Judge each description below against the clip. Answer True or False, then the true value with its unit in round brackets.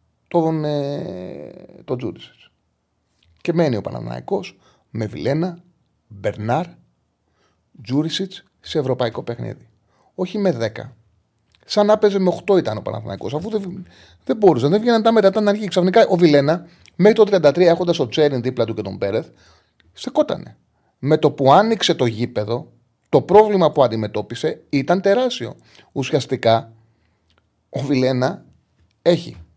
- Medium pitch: True (145 Hz)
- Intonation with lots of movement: True (8.1 semitones)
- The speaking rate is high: False (135 wpm)